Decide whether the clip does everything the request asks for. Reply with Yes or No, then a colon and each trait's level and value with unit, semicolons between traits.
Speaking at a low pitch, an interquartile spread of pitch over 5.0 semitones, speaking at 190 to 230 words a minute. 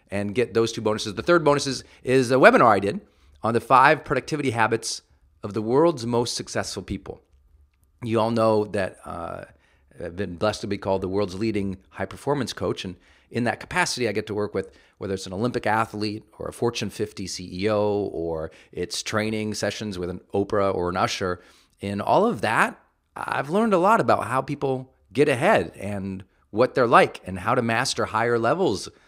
No: low, 105 Hz; average, 3.4 semitones; average, 195 wpm